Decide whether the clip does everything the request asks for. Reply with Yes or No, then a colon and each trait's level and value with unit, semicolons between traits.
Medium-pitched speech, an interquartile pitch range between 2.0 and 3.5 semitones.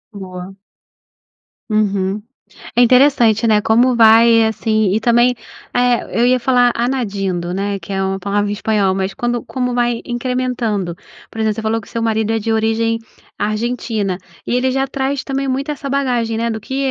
No: high, 225 Hz; average, 3.1 semitones